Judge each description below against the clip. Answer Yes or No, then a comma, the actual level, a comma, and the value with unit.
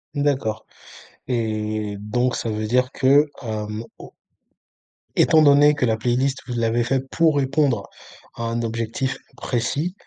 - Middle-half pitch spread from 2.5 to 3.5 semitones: No, average, 3.9 semitones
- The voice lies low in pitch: Yes, low, 120 Hz